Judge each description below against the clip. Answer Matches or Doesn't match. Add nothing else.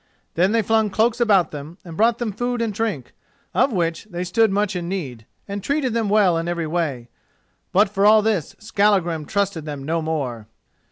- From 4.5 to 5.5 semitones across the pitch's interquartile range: Matches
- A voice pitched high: Matches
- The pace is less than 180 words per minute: Doesn't match